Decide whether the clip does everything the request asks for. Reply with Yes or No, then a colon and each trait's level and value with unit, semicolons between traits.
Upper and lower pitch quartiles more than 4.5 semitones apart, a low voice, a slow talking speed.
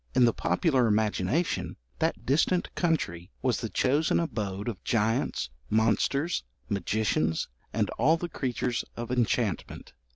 Yes: average, 5.0 semitones; low, 115 Hz; slow, 125 wpm